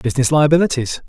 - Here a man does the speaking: Yes, male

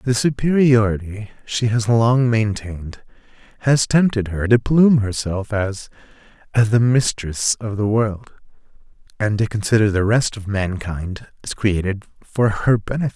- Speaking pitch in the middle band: No, low, 110 Hz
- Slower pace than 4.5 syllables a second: Yes, 4.3 syllables/s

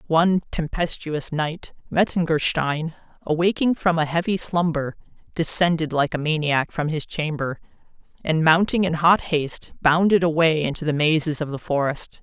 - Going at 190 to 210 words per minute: No, average, 140 wpm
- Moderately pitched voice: Yes, medium, 160 Hz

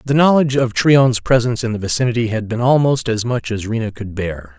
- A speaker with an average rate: No, fast, 225 wpm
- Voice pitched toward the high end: No, low, 115 Hz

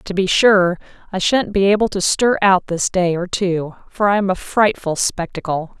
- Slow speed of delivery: No, fast, 205 wpm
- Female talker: Yes, female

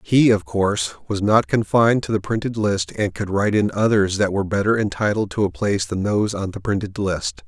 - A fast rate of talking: Yes, fast, 225 wpm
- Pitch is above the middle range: No, low, 105 Hz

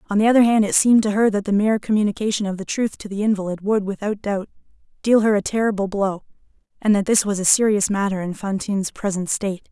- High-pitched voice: Yes, high, 205 Hz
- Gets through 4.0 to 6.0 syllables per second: No, 6.6 syllables/s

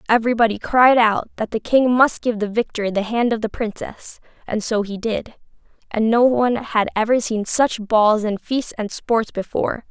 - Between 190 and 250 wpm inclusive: Yes, average, 195 wpm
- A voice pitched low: No, high, 225 Hz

